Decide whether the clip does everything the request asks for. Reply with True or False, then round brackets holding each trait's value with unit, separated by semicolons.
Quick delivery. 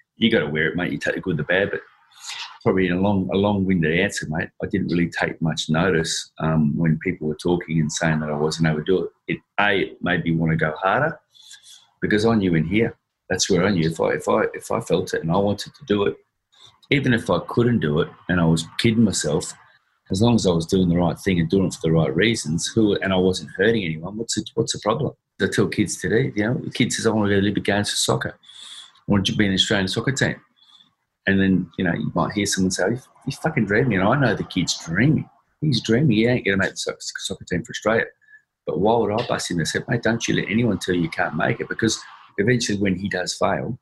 True (260 wpm)